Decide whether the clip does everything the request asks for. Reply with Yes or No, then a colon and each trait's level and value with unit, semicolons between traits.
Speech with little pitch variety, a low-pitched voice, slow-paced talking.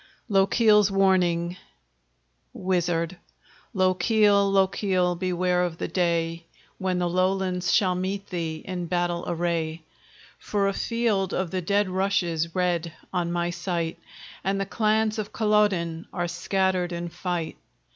No: narrow, 2.2 semitones; medium, 180 Hz; slow, 125 wpm